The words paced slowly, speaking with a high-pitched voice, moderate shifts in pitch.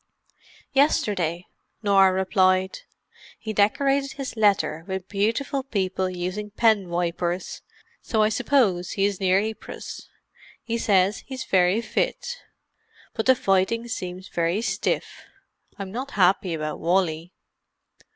Yes: slow, 120 wpm; high, 195 Hz; average, 3.5 semitones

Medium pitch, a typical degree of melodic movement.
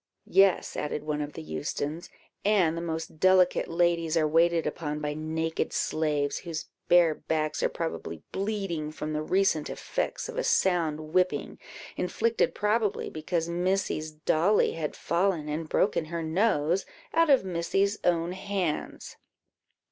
Yes: medium, 170 Hz; average, 3.5 semitones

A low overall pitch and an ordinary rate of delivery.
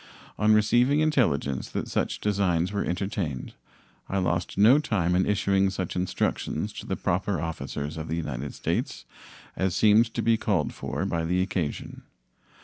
Yes: very low, 95 Hz; average, 155 wpm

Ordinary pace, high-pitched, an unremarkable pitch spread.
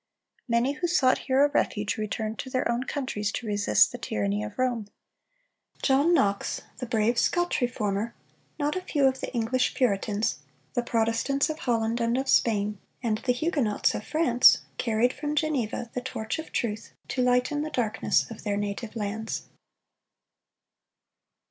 Yes: average, 160 wpm; high, 235 Hz; average, 3.7 semitones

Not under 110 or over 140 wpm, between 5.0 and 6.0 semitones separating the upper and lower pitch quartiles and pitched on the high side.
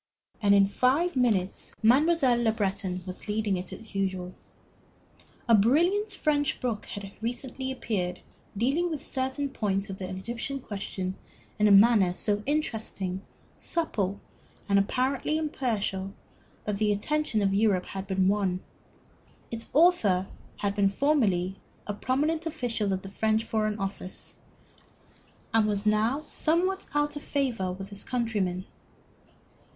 Yes: slow, 135 wpm; wide, 5.4 semitones; high, 215 Hz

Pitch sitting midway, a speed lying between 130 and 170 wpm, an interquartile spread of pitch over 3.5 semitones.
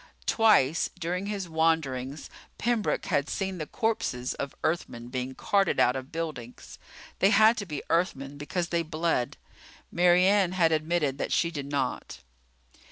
Yes: medium, 165 Hz; average, 150 wpm; average, 4.9 semitones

